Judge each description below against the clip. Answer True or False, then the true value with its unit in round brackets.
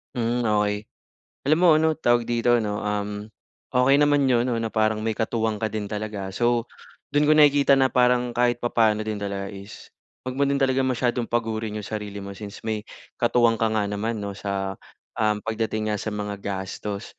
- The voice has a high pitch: False (110 Hz)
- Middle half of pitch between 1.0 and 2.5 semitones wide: False (2.9 semitones)